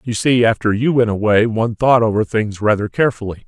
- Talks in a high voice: No, low, 110 Hz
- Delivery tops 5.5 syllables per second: Yes, 6.0 syllables/s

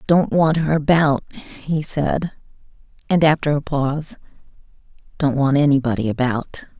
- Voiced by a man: No, female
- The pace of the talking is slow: Yes, slow, 125 wpm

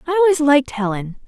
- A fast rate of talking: No, average, 190 wpm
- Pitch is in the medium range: No, very high, 280 Hz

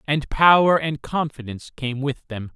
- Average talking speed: Yes, average, 165 wpm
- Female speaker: No, male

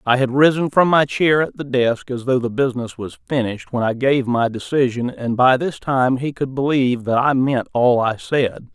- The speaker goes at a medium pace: No, fast, 225 wpm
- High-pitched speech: No, low, 130 Hz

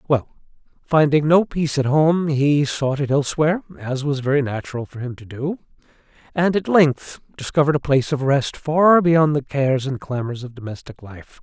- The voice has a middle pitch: Yes, medium, 145 Hz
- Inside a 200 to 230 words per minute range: No, average, 185 wpm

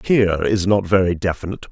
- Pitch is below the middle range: Yes, very low, 95 Hz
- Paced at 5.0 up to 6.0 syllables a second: No, 6.3 syllables/s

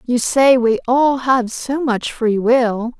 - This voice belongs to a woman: Yes, female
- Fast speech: No, average, 180 wpm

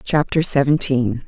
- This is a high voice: No, medium, 140 Hz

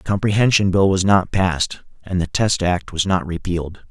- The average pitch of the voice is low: Yes, very low, 95 Hz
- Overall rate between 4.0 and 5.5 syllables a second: Yes, 5.2 syllables/s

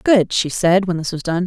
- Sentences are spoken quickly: Yes, fast, 285 wpm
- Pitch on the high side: No, medium, 180 Hz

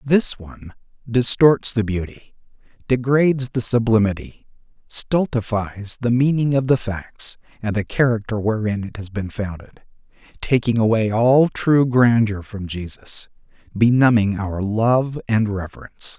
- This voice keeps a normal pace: No, slow, 125 wpm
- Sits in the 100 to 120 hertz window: Yes, low, 115 Hz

